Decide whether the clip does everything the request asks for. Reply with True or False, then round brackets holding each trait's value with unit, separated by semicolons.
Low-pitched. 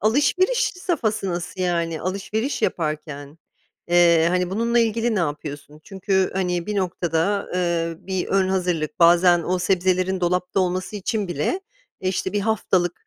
False (185 Hz)